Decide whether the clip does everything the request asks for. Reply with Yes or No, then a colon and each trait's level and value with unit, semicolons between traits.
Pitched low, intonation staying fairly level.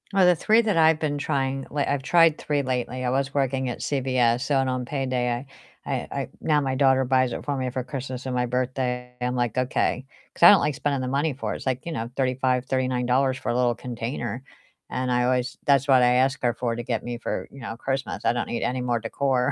Yes: low, 130 Hz; narrow, 1.8 semitones